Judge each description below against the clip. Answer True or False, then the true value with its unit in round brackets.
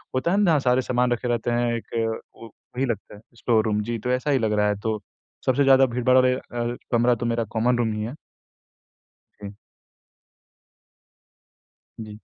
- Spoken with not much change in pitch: True (2.3 semitones)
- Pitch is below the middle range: True (120 Hz)